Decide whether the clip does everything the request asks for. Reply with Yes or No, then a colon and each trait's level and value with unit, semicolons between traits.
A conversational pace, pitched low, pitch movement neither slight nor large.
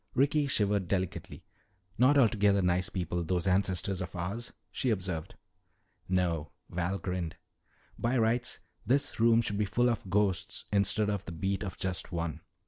Yes: average, 150 wpm; low, 100 Hz; average, 3.9 semitones